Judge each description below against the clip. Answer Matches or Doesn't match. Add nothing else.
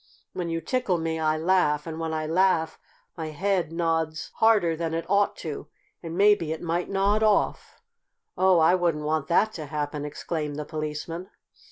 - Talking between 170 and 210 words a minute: Matches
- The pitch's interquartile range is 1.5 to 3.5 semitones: Matches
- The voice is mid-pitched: Matches